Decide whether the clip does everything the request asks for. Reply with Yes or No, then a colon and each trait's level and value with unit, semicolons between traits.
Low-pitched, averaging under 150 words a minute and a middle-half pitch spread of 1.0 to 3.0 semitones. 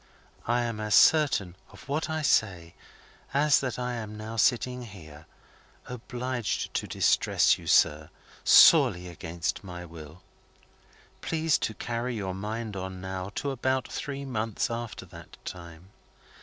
No: low, 110 Hz; average, 140 wpm; wide, 5.4 semitones